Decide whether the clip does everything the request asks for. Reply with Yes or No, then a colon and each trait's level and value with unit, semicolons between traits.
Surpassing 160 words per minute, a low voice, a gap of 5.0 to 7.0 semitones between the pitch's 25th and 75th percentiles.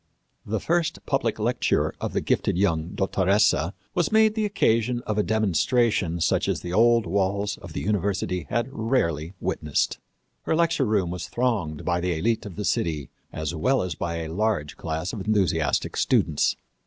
Yes: average, 170 wpm; low, 100 Hz; wide, 5.4 semitones